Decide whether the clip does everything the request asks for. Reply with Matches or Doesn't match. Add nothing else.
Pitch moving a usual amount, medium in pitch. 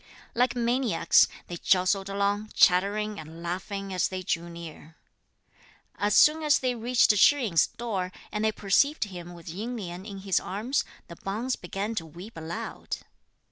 Doesn't match